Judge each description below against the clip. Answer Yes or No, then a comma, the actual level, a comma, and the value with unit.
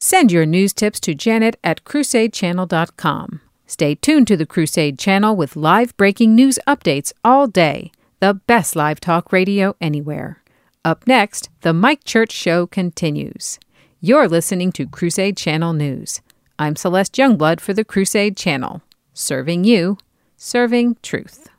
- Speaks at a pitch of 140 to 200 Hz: Yes, high, 190 Hz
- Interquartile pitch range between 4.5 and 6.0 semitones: Yes, wide, 5.5 semitones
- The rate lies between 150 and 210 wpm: No, average, 140 wpm